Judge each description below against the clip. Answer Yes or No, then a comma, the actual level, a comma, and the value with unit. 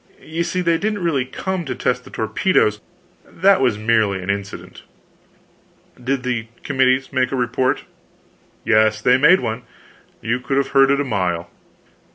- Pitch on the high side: No, low, 130 Hz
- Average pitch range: Yes, average, 4.4 semitones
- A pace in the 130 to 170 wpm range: Yes, average, 160 wpm